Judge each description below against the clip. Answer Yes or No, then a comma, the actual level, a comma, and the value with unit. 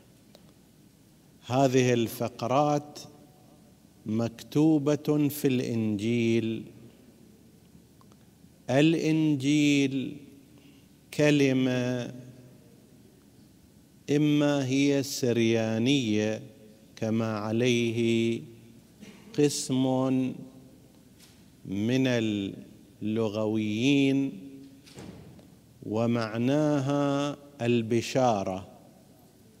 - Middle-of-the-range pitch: No, low, 125 Hz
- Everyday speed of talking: No, slow, 35 wpm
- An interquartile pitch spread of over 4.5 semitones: No, average, 3.8 semitones